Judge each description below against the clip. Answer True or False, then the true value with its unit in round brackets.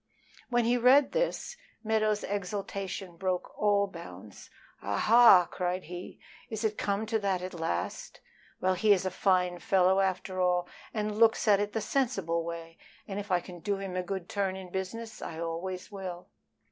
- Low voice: False (190 Hz)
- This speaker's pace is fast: False (175 wpm)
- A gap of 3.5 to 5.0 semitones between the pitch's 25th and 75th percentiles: False (2.9 semitones)